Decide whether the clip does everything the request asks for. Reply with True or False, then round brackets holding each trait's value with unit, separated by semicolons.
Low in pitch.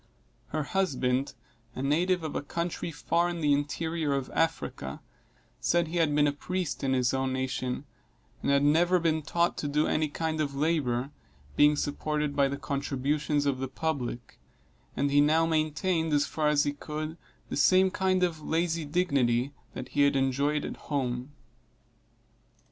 False (150 Hz)